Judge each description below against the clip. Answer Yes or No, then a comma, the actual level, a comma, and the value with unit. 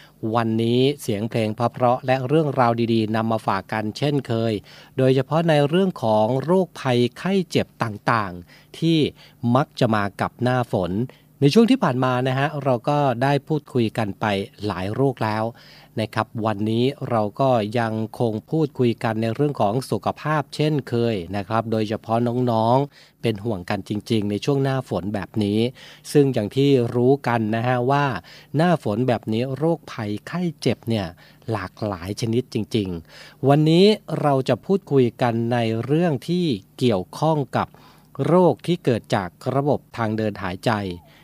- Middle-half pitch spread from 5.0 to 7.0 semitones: No, average, 4.3 semitones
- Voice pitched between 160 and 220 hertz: No, low, 125 Hz